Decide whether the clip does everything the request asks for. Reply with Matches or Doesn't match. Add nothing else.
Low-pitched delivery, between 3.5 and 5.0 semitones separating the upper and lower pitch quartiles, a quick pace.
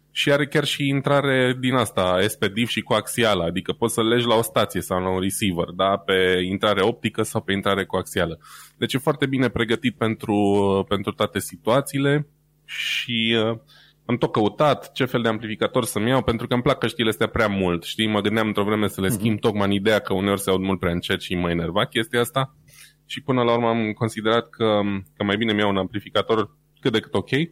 Matches